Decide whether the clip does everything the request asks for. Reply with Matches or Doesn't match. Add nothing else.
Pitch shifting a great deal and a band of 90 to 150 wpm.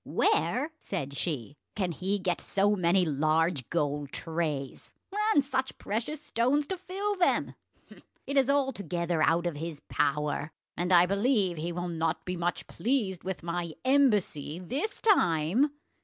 Matches